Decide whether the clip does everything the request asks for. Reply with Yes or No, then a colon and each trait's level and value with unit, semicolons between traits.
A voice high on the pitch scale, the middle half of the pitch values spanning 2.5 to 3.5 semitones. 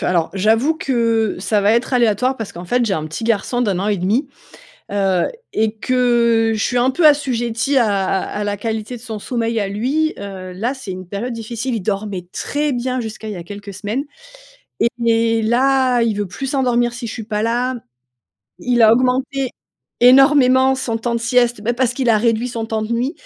Yes: high, 230 Hz; average, 3.2 semitones